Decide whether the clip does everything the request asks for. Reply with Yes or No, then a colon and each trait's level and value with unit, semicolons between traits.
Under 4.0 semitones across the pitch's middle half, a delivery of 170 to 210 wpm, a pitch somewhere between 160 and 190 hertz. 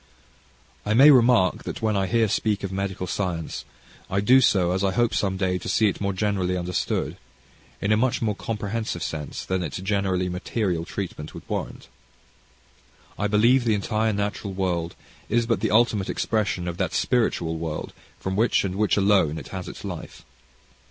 No: average, 3.1 semitones; average, 180 wpm; low, 100 Hz